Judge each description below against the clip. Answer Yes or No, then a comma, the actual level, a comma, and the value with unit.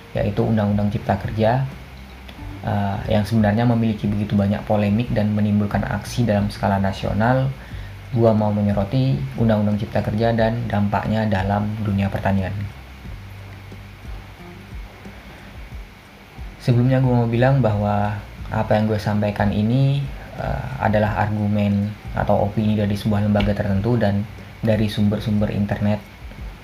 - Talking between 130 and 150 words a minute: No, average, 115 wpm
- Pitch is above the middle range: No, low, 105 Hz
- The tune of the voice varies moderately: No, narrow, 1.7 semitones